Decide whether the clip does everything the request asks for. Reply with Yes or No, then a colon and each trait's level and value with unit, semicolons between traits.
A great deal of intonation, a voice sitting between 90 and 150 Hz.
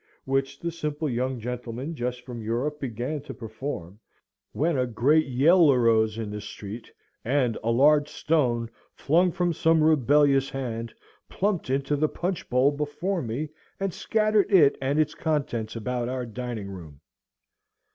No: average, 4.5 semitones; low, 135 Hz